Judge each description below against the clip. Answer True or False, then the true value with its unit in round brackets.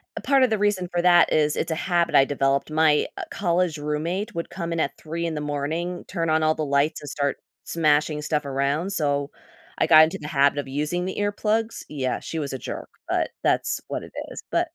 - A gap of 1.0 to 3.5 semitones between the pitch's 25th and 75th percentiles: True (3.2 semitones)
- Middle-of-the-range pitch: True (155 Hz)